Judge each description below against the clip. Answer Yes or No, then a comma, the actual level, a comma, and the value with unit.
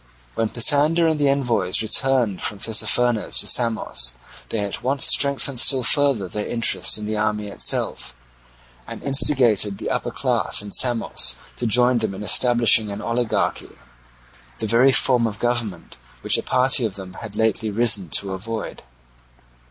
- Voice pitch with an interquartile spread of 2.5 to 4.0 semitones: Yes, average, 3.3 semitones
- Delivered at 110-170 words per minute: Yes, average, 155 wpm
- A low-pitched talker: Yes, low, 115 Hz